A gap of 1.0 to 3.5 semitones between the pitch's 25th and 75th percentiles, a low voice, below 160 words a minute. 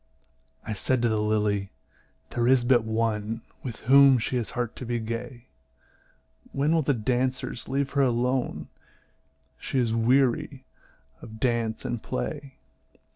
Yes: average, 2.9 semitones; low, 120 Hz; average, 140 wpm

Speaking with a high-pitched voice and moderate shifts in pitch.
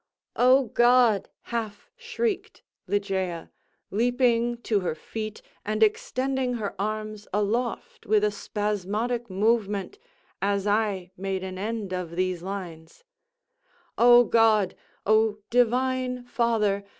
Yes: high, 215 Hz; average, 3.5 semitones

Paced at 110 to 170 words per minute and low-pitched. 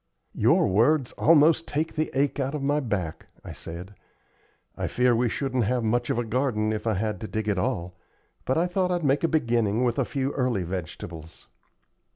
No: average, 195 wpm; low, 120 Hz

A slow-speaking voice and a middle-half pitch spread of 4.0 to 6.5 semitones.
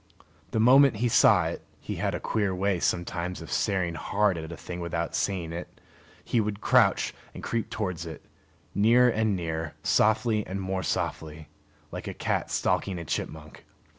No: average, 170 wpm; average, 4.3 semitones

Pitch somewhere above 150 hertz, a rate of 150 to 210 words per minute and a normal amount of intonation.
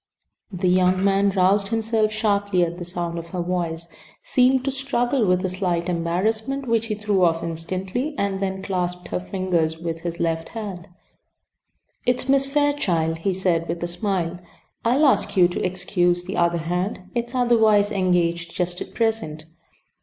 Yes: medium, 185 Hz; average, 165 wpm; average, 4.1 semitones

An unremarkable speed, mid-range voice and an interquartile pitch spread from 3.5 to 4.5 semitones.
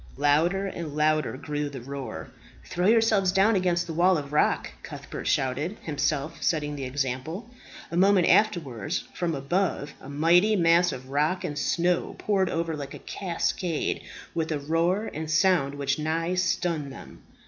Yes: average, 160 wpm; medium, 160 Hz; average, 4.0 semitones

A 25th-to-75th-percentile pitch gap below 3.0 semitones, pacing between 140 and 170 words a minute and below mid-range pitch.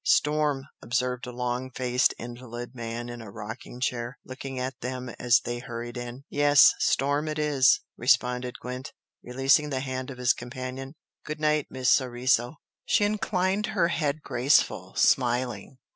Yes: narrow, 2.6 semitones; average, 150 wpm; low, 130 Hz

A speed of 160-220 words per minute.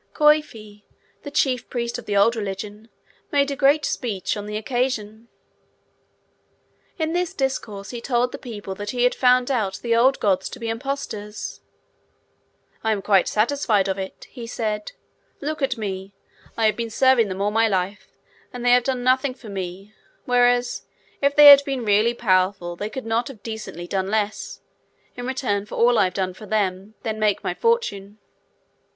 Yes: average, 180 wpm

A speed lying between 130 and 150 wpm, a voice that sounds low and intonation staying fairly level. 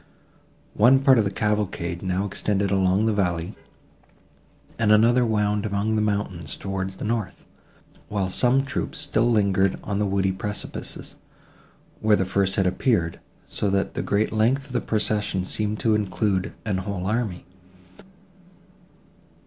Yes: average, 145 wpm; low, 105 Hz; narrow, 2.3 semitones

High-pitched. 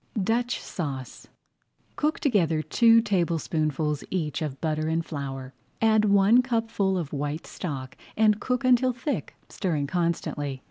No: medium, 170 Hz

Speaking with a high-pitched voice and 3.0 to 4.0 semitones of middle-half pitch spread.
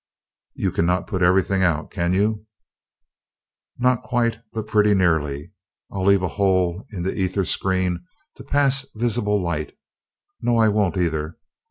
No: very low, 95 Hz; average, 3.4 semitones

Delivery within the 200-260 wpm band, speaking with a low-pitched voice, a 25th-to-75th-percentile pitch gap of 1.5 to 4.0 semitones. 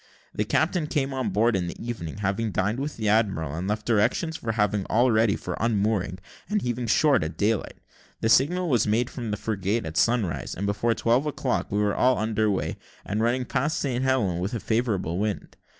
Yes: fast, 205 wpm; low, 110 Hz; average, 3.4 semitones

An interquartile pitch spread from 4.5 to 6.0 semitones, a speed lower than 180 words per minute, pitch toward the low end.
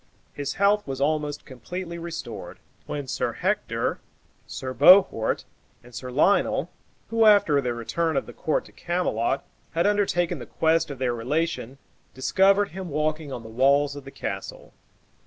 No: average, 4.8 semitones; average, 155 wpm; medium, 150 Hz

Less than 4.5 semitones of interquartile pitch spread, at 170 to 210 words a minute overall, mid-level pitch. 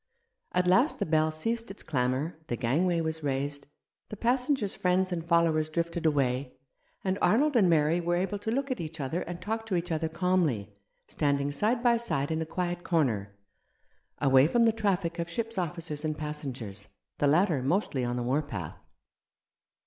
No: average, 4.8 semitones; average, 180 wpm; medium, 165 Hz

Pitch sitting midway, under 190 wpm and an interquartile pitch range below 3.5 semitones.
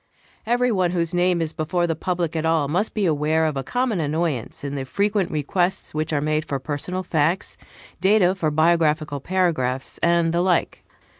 Yes: medium, 165 Hz; average, 180 wpm; average, 3.1 semitones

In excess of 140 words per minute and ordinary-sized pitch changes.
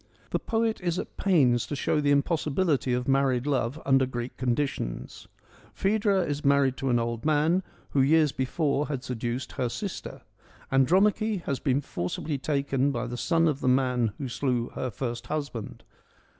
Yes: average, 165 wpm; average, 3.7 semitones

